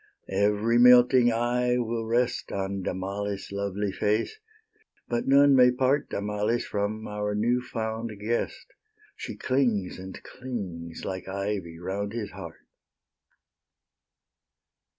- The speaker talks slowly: Yes, slow, 110 wpm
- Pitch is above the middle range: No, low, 105 Hz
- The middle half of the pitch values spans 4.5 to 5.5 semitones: No, average, 3.5 semitones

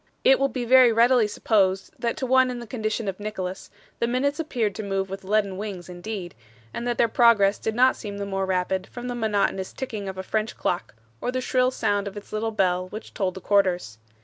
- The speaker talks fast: Yes, fast, 225 wpm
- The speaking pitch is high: Yes, high, 215 Hz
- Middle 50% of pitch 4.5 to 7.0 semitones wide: No, average, 3.9 semitones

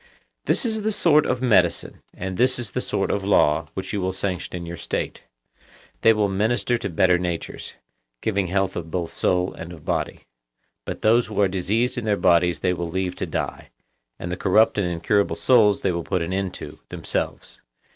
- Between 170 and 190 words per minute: No, average, 200 wpm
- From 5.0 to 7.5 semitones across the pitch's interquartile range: No, average, 3.7 semitones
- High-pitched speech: No, very low, 95 Hz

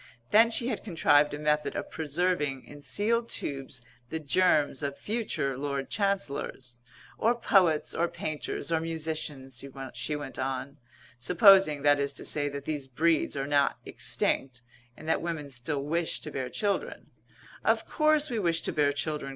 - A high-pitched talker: No, medium, 150 Hz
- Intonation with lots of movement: No, average, 3.8 semitones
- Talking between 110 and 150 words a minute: No, average, 165 wpm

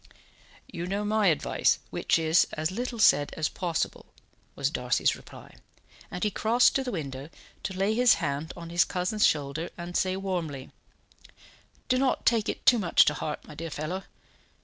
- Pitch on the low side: No, medium, 180 Hz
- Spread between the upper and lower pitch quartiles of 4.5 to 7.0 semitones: Yes, average, 5.1 semitones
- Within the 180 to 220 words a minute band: No, average, 170 wpm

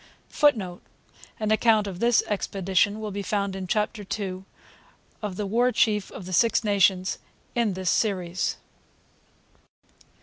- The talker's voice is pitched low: No, high, 205 Hz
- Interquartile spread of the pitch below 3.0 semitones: Yes, narrow, 2.5 semitones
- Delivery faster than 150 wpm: No, slow, 135 wpm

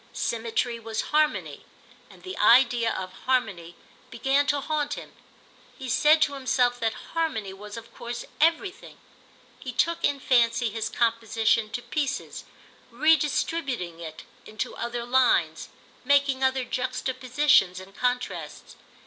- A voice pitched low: No, very high, 250 Hz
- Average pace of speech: No, slow, 125 wpm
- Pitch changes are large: No, average, 3.8 semitones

